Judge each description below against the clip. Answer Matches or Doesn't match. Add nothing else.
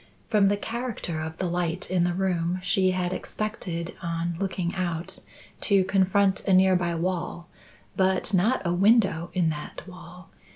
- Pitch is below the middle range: Doesn't match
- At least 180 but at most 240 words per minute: Doesn't match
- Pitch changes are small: Matches